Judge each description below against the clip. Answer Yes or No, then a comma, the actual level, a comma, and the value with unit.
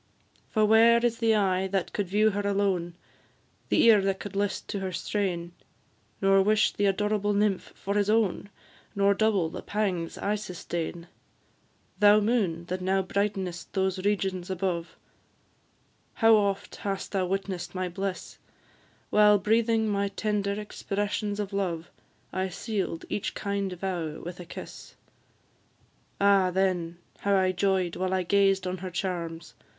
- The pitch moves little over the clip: Yes, narrow, 2.1 semitones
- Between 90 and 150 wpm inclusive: Yes, average, 145 wpm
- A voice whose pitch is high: Yes, high, 195 Hz